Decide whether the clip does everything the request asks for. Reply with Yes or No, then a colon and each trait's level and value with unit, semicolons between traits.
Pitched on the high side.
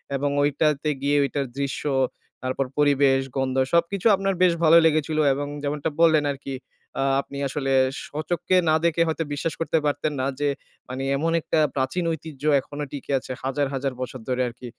No: medium, 145 Hz